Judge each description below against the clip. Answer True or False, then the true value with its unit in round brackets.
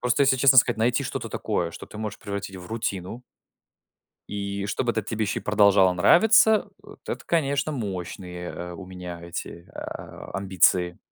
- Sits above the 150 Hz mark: False (100 Hz)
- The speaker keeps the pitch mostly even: False (5.0 semitones)